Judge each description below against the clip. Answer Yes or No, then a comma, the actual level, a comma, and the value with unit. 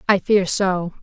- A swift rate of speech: No, average, 175 wpm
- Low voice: No, high, 190 Hz